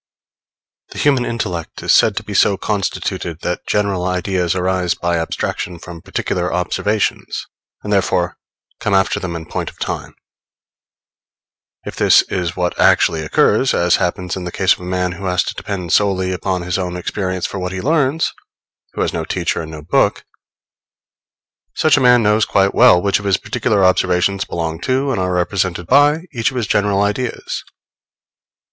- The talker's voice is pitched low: Yes, very low, 95 Hz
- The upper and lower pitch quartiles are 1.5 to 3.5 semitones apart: Yes, narrow, 2.6 semitones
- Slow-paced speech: No, average, 175 wpm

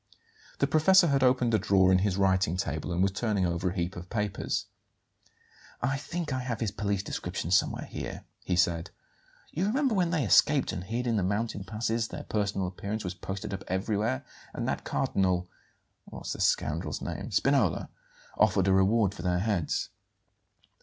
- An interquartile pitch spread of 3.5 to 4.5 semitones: Yes, average, 4.1 semitones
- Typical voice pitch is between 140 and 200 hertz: No, low, 100 Hz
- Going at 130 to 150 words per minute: No, average, 175 wpm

